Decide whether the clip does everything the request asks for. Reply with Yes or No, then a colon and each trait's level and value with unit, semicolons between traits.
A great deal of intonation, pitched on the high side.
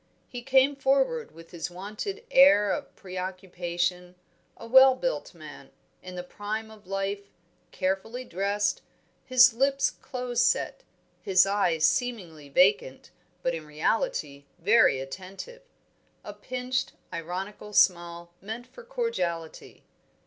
Yes: wide, 6.3 semitones; high, 205 Hz